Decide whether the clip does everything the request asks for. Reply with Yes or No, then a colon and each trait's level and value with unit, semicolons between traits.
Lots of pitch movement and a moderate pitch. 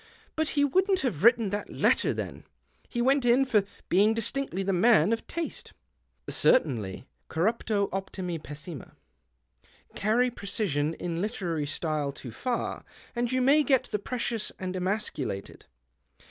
No: wide, 6.2 semitones; high, 210 Hz